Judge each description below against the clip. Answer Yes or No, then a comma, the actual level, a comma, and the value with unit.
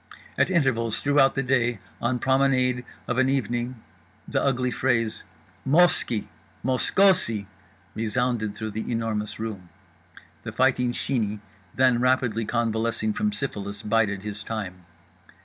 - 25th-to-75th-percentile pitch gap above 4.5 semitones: No, average, 3.2 semitones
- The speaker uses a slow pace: Yes, slow, 125 wpm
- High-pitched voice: No, low, 120 Hz